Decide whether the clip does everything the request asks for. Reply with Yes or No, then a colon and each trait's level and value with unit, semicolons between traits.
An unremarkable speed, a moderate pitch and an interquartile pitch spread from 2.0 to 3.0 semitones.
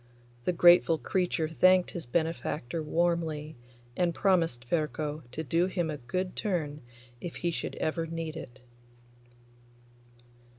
No: slow, 125 wpm; medium, 165 Hz; narrow, 2.4 semitones